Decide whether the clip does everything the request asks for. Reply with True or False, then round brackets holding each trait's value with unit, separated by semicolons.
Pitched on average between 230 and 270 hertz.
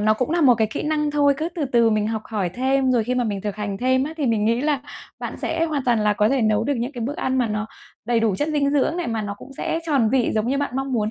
True (250 Hz)